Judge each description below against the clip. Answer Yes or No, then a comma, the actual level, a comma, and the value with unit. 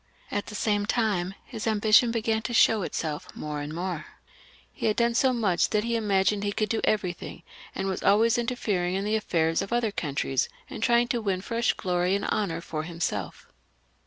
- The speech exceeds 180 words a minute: Yes, average, 190 wpm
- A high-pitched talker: Yes, high, 205 Hz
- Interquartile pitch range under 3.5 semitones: No, average, 4.0 semitones